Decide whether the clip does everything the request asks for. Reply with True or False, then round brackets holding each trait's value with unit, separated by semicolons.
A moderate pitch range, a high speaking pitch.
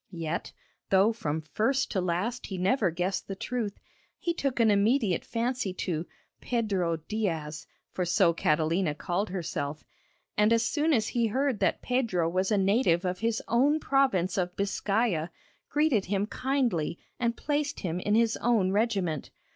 True (5.0 semitones; 205 Hz)